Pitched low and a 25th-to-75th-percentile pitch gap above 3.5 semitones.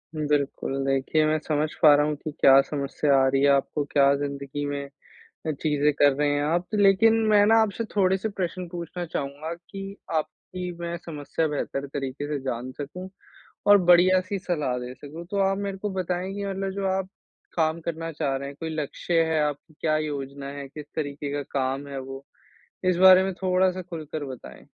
No: medium, 155 Hz; average, 4.5 semitones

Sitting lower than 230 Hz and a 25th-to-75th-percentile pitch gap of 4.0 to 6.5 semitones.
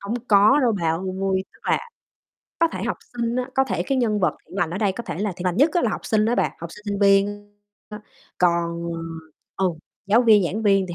No: high, 205 Hz; average, 3.5 semitones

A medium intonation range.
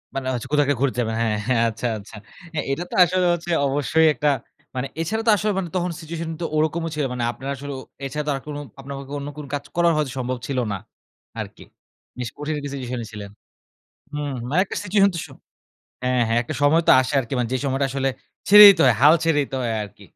Yes: average, 4.2 semitones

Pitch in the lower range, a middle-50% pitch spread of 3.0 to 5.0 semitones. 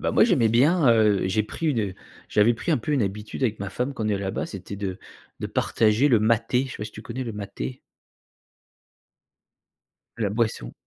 Yes: low, 110 Hz; average, 3.4 semitones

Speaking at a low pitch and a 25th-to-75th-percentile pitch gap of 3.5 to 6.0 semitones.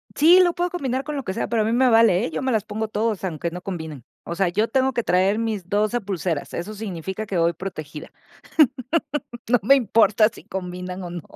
No: high, 210 Hz; average, 4.4 semitones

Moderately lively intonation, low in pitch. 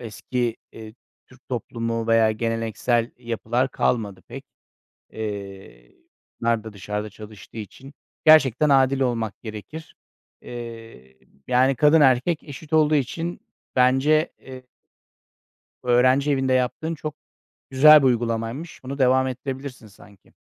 Yes: average, 3.2 semitones; low, 125 Hz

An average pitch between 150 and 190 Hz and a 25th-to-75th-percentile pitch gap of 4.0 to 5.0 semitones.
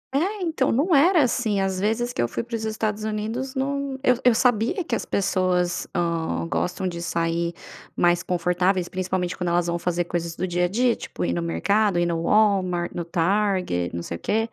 Yes: medium, 185 Hz; average, 4.7 semitones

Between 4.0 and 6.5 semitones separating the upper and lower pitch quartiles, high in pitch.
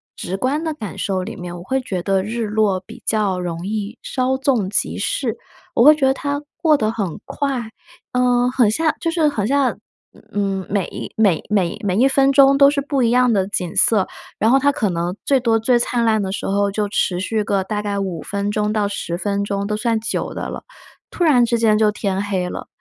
Yes: average, 4.5 semitones; high, 215 Hz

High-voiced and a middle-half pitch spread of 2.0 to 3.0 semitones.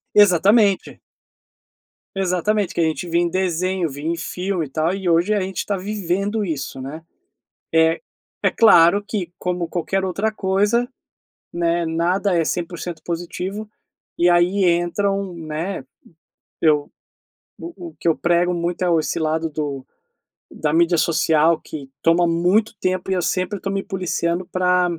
No: medium, 175 Hz; average, 2.7 semitones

